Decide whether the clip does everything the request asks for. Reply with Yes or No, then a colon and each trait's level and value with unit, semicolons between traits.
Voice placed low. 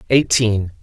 Yes: low, 110 Hz